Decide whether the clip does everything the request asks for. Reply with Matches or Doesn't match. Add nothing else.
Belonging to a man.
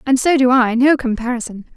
Doesn't match